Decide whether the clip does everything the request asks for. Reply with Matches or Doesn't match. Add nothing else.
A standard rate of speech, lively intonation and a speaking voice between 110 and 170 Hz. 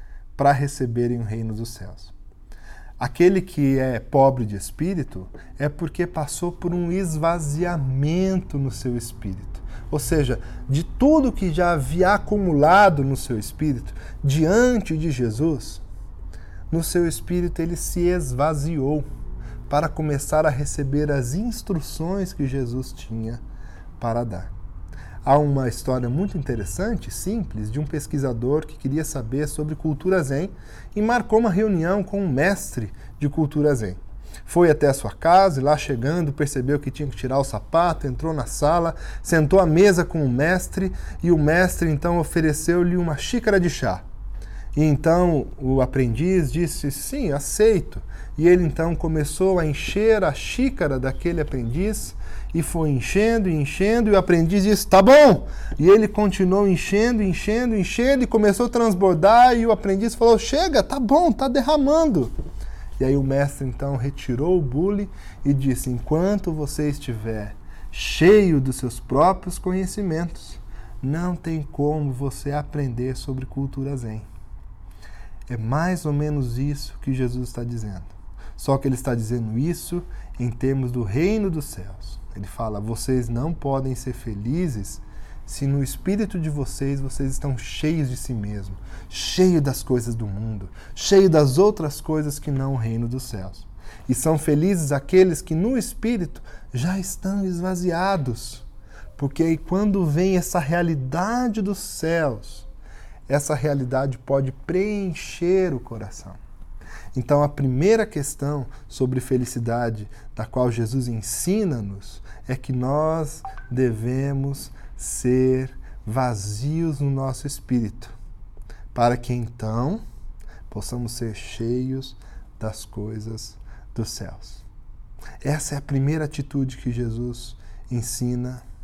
Matches